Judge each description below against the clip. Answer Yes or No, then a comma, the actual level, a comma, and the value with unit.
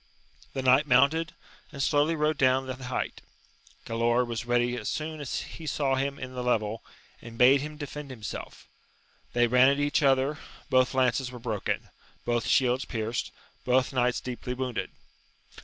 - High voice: No, low, 130 Hz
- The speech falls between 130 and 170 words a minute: Yes, average, 160 wpm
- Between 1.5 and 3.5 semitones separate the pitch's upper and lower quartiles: Yes, narrow, 2.5 semitones